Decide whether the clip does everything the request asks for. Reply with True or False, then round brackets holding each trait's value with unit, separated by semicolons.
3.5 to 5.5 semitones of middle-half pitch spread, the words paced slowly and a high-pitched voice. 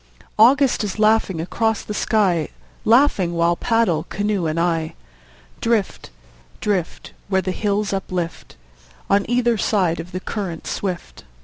True (4.2 semitones; 130 wpm; 195 Hz)